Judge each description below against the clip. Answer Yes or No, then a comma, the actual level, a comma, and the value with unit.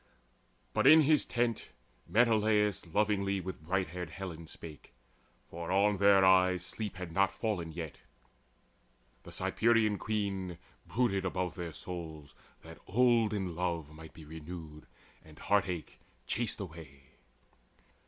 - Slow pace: Yes, slow, 125 wpm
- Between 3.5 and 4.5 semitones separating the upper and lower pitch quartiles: Yes, average, 4.1 semitones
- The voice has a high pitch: No, very low, 95 Hz